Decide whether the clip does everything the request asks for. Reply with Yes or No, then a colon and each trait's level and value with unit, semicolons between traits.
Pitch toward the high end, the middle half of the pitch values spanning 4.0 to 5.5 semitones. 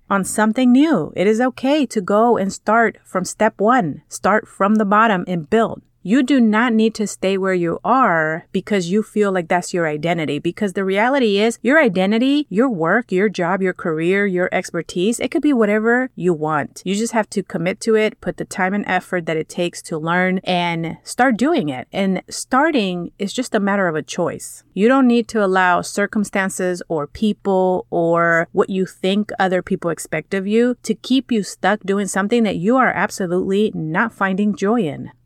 No: high, 200 Hz; average, 3.6 semitones